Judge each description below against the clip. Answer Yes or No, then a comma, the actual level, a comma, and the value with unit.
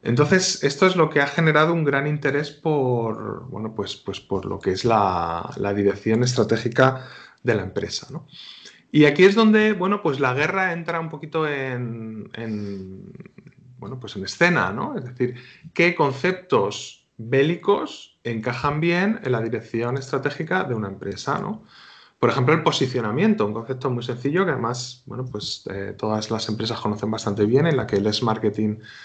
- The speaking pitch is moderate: No, low, 125 Hz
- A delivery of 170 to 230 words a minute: Yes, average, 175 wpm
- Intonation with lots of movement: Yes, wide, 6.2 semitones